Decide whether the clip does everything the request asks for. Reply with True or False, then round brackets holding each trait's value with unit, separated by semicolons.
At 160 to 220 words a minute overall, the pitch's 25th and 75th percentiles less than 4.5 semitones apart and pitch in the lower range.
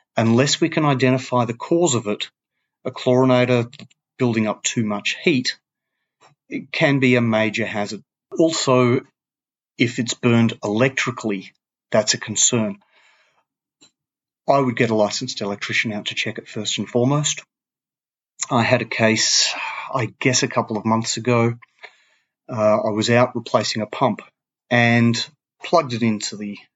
False (145 wpm; 2.9 semitones; 120 Hz)